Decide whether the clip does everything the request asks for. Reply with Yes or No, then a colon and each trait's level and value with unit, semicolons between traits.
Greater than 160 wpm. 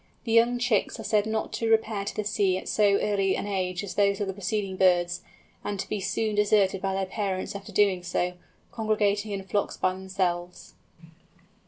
Yes: average, 195 wpm